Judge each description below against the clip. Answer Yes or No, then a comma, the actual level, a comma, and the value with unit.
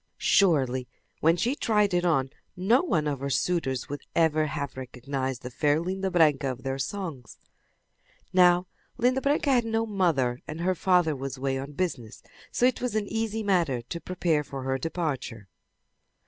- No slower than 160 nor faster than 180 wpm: Yes, average, 170 wpm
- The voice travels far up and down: Yes, wide, 6.1 semitones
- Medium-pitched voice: Yes, medium, 160 Hz